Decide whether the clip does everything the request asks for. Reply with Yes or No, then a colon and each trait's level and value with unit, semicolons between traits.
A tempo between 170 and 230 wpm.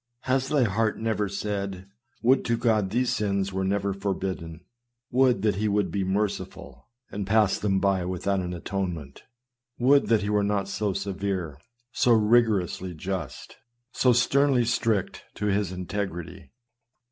No: average, 160 wpm